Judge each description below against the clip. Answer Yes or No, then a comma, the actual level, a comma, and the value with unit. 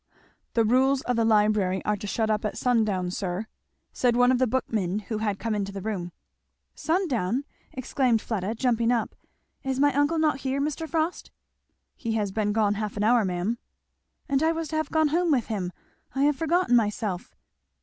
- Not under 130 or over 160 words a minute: No, average, 190 wpm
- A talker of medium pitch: No, high, 230 Hz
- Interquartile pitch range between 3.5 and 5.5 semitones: Yes, average, 4.8 semitones